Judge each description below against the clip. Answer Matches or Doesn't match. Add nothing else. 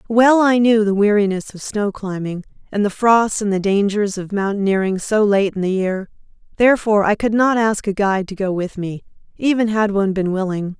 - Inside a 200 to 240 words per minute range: Matches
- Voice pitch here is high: Matches